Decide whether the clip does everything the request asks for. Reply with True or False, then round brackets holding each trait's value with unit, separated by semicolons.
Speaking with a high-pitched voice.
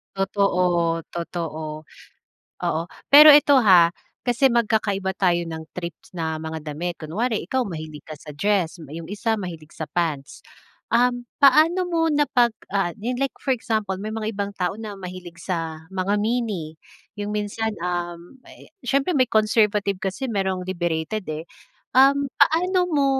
True (195 Hz)